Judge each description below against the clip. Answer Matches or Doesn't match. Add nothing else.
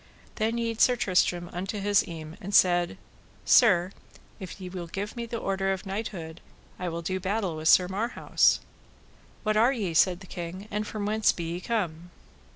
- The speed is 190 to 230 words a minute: Doesn't match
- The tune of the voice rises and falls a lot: Doesn't match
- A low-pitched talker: Doesn't match